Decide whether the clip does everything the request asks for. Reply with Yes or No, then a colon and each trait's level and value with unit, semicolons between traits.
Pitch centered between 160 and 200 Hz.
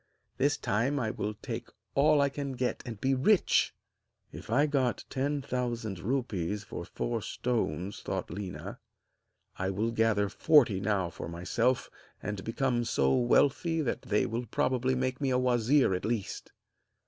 No: low, 120 Hz